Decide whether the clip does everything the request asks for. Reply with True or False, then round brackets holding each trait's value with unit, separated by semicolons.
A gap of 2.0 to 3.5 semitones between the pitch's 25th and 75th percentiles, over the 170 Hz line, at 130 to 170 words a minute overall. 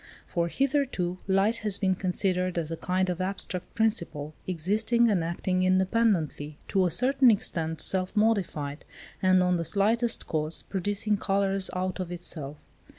True (3.2 semitones; 185 Hz; 150 wpm)